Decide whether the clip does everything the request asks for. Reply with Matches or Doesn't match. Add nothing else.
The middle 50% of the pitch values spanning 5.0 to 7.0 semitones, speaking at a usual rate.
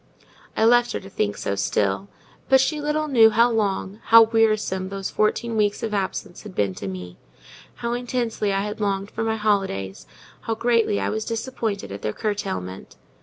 Doesn't match